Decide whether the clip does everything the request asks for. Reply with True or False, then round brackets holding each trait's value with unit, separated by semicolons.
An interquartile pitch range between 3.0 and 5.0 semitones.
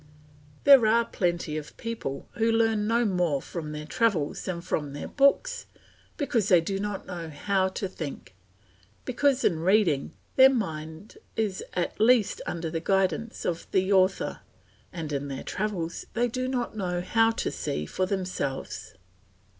False (5.6 semitones)